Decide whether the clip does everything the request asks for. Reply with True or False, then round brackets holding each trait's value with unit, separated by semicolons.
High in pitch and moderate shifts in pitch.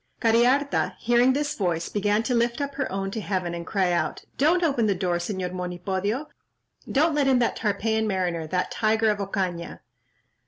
True (210 Hz; 5.0 semitones)